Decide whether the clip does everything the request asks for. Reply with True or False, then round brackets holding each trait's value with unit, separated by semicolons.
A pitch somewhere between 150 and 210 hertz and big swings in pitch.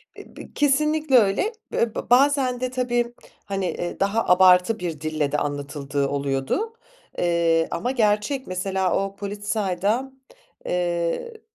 True (195 Hz; 6.6 semitones)